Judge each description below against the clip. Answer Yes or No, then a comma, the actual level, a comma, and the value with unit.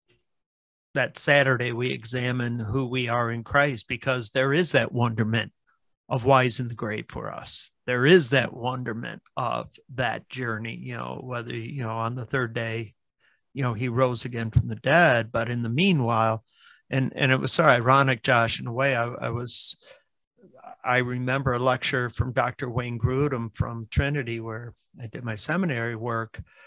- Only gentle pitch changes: Yes, narrow, 2.3 semitones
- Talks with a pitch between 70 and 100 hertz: No, low, 125 Hz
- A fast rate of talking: No, average, 175 wpm